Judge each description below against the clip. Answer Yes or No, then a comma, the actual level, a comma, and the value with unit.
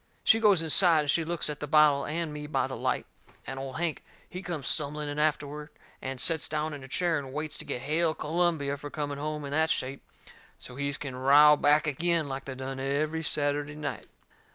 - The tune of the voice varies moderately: No, narrow, 2.0 semitones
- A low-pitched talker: No, medium, 150 Hz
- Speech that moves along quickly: Yes, fast, 215 wpm